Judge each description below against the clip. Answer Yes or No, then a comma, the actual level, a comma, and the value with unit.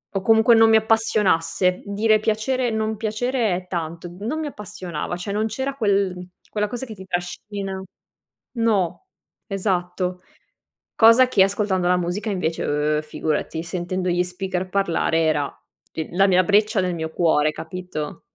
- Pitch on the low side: No, high, 190 Hz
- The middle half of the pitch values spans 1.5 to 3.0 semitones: No, average, 3.5 semitones